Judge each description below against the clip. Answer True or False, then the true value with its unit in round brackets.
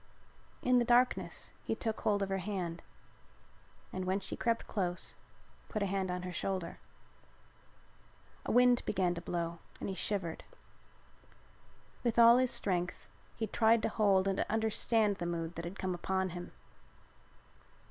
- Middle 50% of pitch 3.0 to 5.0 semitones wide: True (3.8 semitones)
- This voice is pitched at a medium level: False (195 Hz)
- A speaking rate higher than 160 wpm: False (155 wpm)